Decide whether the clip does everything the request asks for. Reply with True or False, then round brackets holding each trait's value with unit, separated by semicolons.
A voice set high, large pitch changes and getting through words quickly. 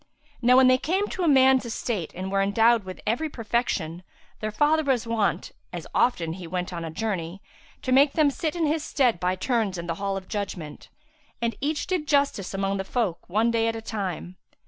True (225 Hz; 5.9 semitones; 210 wpm)